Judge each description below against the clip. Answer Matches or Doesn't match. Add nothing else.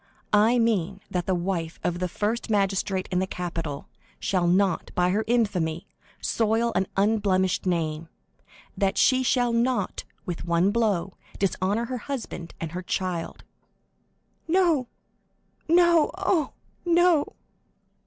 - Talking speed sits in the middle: Doesn't match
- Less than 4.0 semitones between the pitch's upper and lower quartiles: Doesn't match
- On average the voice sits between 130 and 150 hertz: Doesn't match